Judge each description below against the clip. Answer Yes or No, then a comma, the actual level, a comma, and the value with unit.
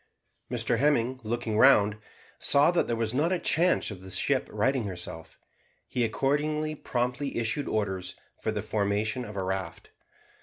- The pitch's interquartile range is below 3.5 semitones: No, average, 5.2 semitones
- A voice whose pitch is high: No, low, 115 Hz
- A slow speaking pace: No, average, 155 wpm